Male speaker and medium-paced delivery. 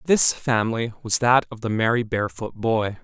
Yes: male; average, 180 wpm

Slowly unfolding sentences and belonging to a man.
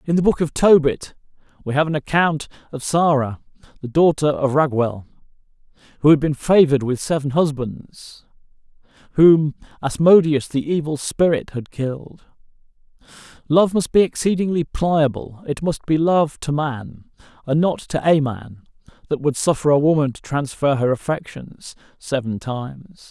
No: average, 145 wpm; male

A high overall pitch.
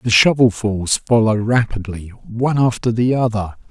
No: low, 110 Hz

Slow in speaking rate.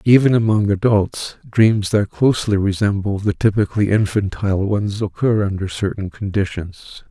Yes: slow, 125 wpm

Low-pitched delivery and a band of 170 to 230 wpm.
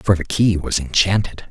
Yes: very low, 90 Hz; average, 200 wpm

